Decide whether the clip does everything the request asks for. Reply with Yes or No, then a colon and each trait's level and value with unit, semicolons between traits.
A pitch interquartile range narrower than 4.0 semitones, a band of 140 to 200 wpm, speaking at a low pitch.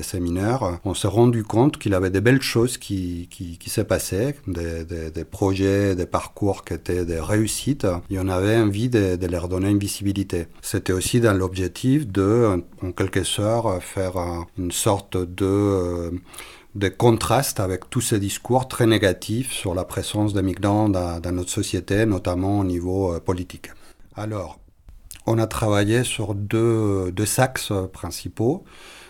Yes: average, 3.4 semitones; average, 160 wpm; very low, 95 Hz